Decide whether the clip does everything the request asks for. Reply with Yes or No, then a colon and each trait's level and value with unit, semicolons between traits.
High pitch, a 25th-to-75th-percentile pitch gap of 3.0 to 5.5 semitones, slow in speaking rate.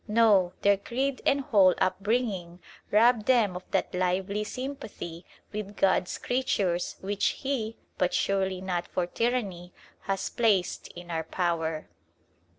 Yes: high, 195 Hz; average, 4.1 semitones; slow, 130 wpm